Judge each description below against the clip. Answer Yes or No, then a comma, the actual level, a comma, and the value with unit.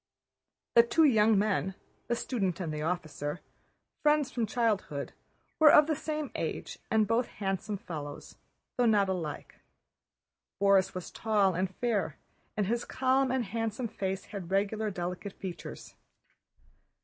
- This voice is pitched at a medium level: No, high, 205 Hz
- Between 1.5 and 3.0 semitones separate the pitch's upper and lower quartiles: No, average, 4.1 semitones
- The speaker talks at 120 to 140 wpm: Yes, slow, 135 wpm